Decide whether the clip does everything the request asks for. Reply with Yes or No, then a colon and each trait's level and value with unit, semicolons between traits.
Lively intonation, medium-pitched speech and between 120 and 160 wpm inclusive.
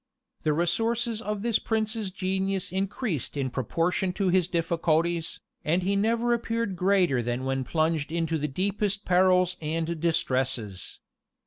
No: average, 4.1 semitones; medium, 180 Hz; slow, 135 wpm